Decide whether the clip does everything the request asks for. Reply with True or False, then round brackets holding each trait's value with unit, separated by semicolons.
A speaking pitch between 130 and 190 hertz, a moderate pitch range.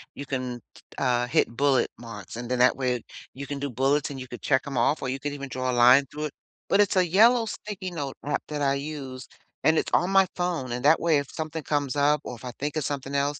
True (140 Hz; 3.0 semitones)